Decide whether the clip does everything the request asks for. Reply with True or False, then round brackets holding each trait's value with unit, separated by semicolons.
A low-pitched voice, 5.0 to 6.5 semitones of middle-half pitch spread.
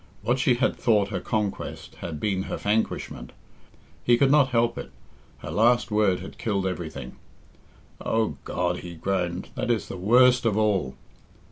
False (105 Hz; 4.6 semitones)